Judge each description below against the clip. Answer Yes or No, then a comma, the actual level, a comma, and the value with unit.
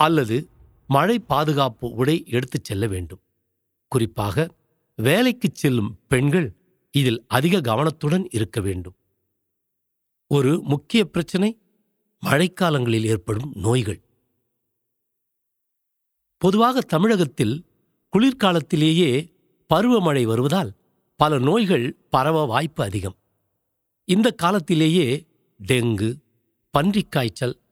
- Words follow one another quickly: No, average, 80 wpm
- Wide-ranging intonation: Yes, wide, 7.2 semitones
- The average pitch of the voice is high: No, medium, 140 Hz